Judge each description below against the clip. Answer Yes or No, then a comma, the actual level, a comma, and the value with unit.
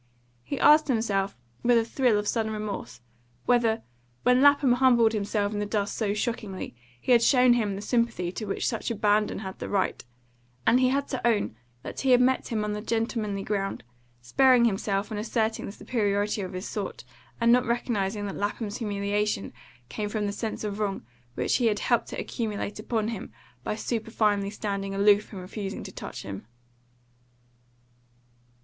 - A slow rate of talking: No, average, 175 wpm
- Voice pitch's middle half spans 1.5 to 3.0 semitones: Yes, narrow, 2.6 semitones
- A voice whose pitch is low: No, high, 215 Hz